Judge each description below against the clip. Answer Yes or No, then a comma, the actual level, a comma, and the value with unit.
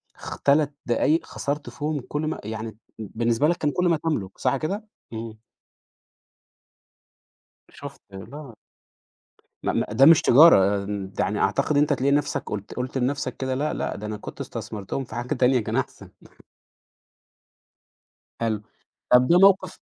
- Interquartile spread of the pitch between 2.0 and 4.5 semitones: No, average, 5.3 semitones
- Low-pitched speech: Yes, low, 130 Hz